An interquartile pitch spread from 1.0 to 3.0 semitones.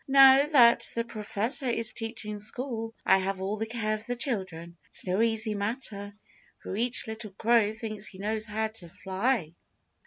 Yes: narrow, 2.5 semitones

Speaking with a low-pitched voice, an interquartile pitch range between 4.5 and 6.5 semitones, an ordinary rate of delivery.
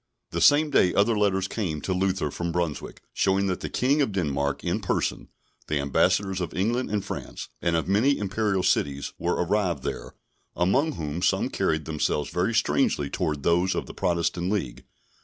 No: very low, 90 Hz; average, 4.1 semitones; average, 175 wpm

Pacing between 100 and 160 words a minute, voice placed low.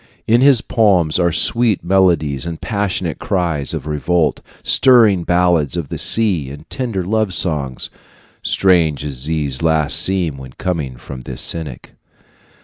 Yes: average, 140 wpm; very low, 85 Hz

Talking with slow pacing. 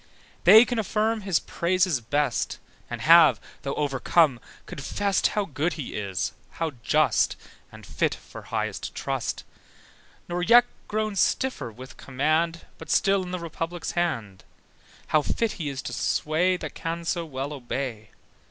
No: average, 145 wpm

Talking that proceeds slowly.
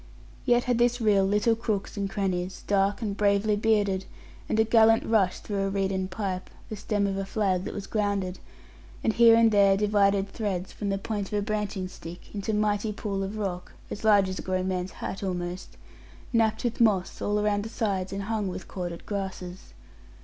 No: average, 195 wpm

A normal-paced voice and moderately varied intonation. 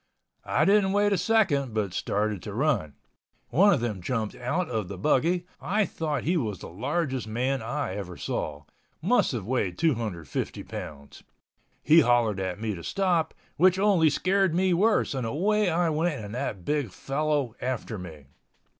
No: average, 165 wpm; wide, 8.5 semitones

